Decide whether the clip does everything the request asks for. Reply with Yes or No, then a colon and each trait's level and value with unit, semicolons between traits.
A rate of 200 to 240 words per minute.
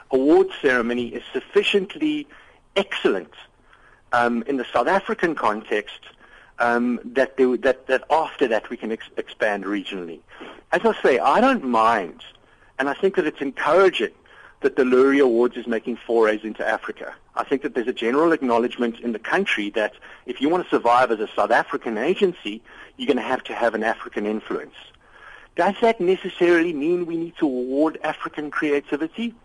No: average, 175 wpm